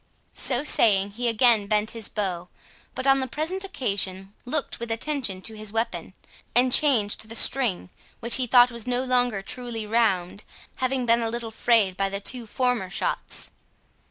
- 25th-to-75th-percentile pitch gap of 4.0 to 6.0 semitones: No, average, 3.6 semitones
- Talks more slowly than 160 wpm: No, average, 170 wpm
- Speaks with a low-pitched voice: No, high, 230 Hz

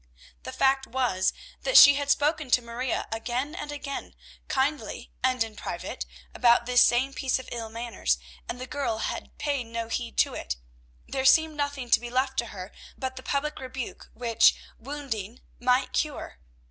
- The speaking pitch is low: No, very high, 255 Hz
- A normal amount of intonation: Yes, average, 3.1 semitones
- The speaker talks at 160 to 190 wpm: Yes, average, 170 wpm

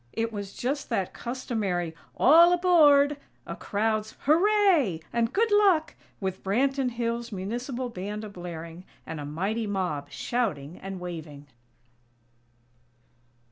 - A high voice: Yes, high, 225 Hz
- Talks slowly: Yes, slow, 120 wpm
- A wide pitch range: Yes, wide, 6.9 semitones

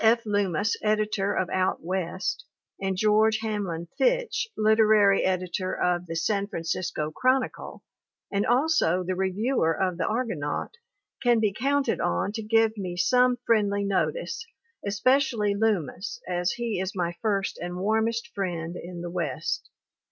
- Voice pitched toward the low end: No, high, 200 Hz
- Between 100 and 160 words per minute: Yes, average, 140 wpm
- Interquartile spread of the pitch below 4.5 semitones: Yes, average, 3.7 semitones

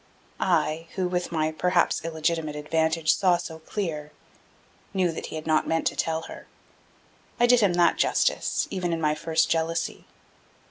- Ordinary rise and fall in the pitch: No, narrow, 1.8 semitones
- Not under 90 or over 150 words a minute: No, average, 165 wpm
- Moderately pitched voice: Yes, medium, 165 Hz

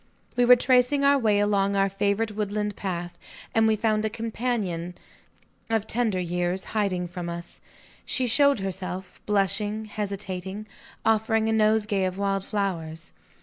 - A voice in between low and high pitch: No, high, 205 Hz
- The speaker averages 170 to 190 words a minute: No, average, 145 wpm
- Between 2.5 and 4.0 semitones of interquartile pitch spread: Yes, average, 2.8 semitones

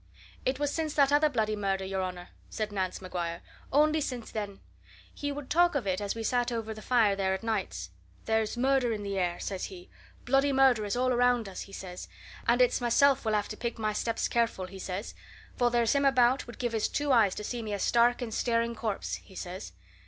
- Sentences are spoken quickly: Yes, fast, 225 wpm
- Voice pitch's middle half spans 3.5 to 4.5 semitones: Yes, average, 4.2 semitones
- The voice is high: Yes, high, 230 Hz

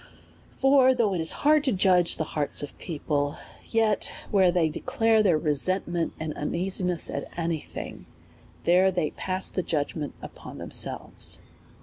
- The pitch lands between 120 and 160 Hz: No, medium, 180 Hz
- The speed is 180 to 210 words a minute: No, average, 160 wpm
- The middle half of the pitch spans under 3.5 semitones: No, average, 4.4 semitones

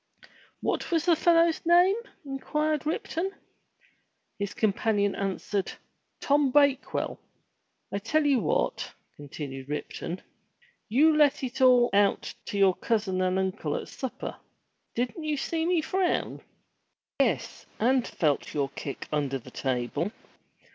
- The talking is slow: Yes, slow, 125 wpm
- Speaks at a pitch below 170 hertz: No, high, 245 Hz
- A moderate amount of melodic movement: No, wide, 8.6 semitones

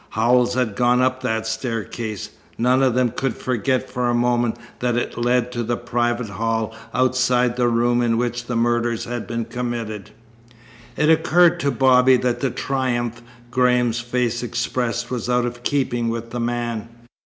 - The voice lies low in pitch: Yes, low, 120 Hz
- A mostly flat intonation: Yes, narrow, 1.3 semitones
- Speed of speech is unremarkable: Yes, average, 165 wpm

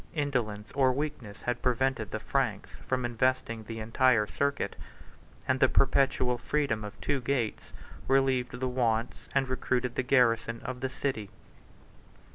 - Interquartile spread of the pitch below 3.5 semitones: Yes, average, 2.7 semitones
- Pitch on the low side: Yes, low, 125 Hz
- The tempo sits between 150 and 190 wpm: No, average, 140 wpm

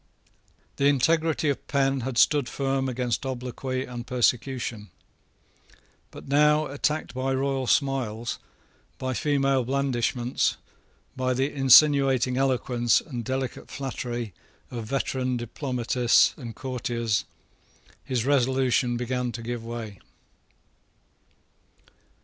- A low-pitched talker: Yes, low, 130 Hz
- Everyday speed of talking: No, slow, 105 wpm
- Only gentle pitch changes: Yes, narrow, 2.1 semitones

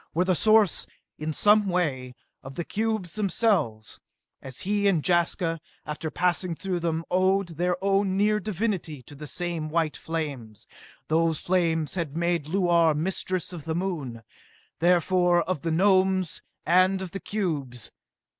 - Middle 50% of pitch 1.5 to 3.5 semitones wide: Yes, average, 3.1 semitones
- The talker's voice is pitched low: No, medium, 175 Hz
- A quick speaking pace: No, average, 145 wpm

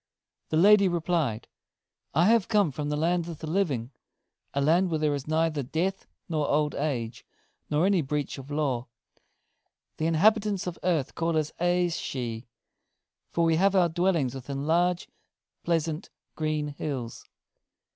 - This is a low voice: No, medium, 160 Hz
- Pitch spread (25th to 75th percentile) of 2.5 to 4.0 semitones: Yes, average, 3.5 semitones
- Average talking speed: Yes, average, 150 wpm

